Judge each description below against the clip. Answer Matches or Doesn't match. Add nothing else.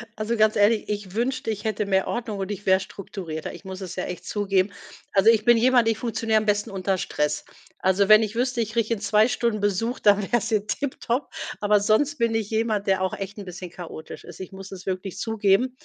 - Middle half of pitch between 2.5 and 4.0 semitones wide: Matches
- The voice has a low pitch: Doesn't match